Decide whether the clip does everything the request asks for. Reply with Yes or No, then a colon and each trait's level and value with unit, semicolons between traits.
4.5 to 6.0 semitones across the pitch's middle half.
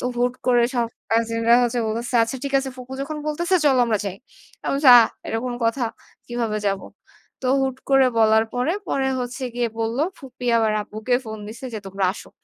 No: average, 2.8 semitones